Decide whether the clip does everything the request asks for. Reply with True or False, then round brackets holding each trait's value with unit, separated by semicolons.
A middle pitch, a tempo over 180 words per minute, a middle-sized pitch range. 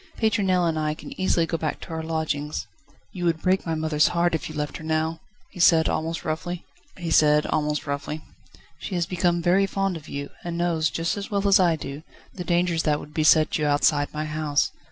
False (160 Hz; 195 wpm; 2.3 semitones)